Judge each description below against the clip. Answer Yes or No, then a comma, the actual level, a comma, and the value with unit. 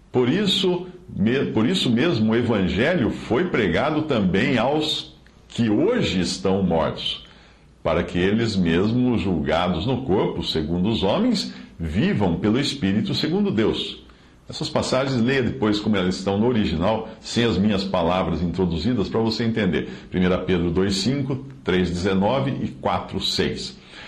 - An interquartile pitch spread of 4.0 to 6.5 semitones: Yes, wide, 5.4 semitones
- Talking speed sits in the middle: Yes, average, 130 wpm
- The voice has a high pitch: No, low, 105 Hz